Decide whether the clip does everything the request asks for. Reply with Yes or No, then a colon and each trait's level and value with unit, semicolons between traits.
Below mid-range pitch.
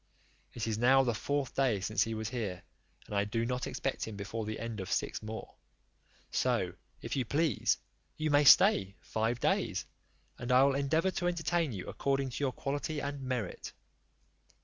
Yes: low, 125 Hz